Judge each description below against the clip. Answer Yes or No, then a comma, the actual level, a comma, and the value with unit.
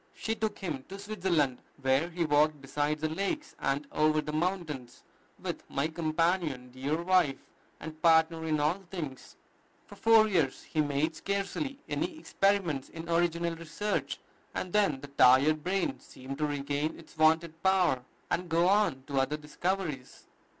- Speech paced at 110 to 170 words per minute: Yes, average, 155 wpm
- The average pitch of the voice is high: No, medium, 160 Hz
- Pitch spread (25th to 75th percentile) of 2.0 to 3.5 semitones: No, average, 3.9 semitones